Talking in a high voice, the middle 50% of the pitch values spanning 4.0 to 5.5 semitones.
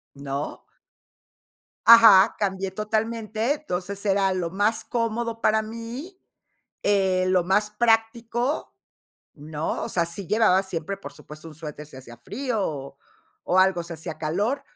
Yes: high, 195 Hz; average, 4.9 semitones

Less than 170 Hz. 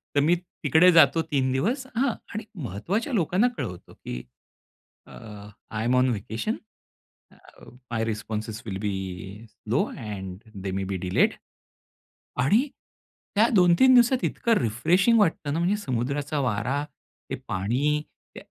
Yes: medium, 140 Hz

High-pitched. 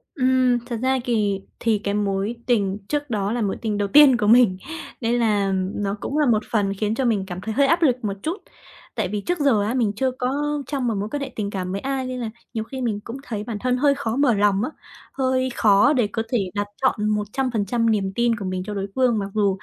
Yes: high, 225 Hz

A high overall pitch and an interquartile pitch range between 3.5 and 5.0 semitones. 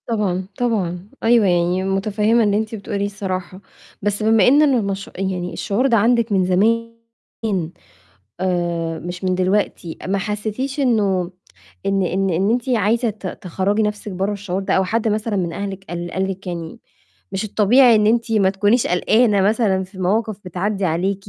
No: high, 200 Hz; average, 2.9 semitones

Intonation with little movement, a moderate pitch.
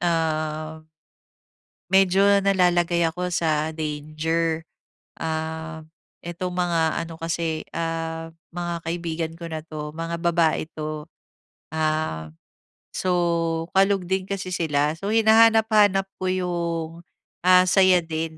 Yes: narrow, 2.2 semitones; medium, 165 Hz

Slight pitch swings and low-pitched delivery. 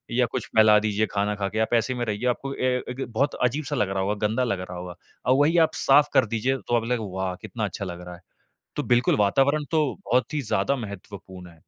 No: average, 4.4 semitones; low, 110 Hz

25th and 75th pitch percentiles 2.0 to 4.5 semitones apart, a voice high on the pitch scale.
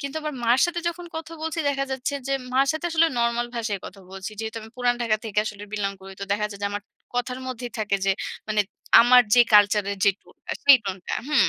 No: average, 4.9 semitones; high, 235 Hz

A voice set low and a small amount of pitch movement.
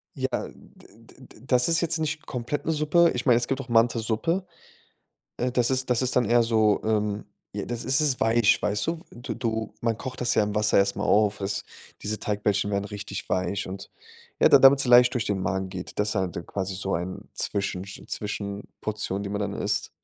No: low, 110 Hz; average, 3.7 semitones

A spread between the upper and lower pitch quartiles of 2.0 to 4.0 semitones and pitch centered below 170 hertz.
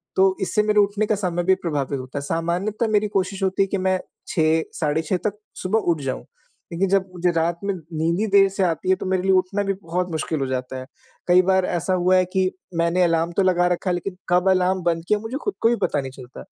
No: average, 2.7 semitones; medium, 180 Hz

